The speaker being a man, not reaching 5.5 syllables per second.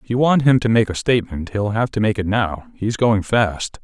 Yes: male; 5.3 syllables/s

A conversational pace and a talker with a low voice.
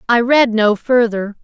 No: average, 165 wpm; high, 230 Hz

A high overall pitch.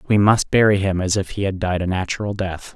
No: very low, 95 Hz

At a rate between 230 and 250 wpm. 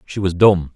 Yes: fast, 235 wpm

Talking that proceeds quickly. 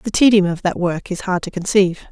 Yes: fast, 255 wpm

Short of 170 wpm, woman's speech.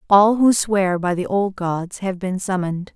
No: fast, 205 wpm; female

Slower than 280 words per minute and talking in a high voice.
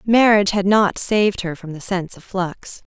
Yes: fast, 205 wpm; high, 195 Hz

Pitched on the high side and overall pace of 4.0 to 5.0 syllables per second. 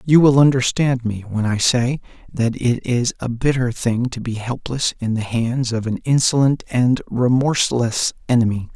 No: low, 125 Hz; 4.6 syllables/s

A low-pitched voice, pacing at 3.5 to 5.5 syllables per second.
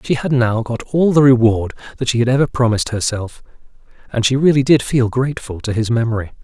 No: low, 120 Hz; 6.1 syllables/s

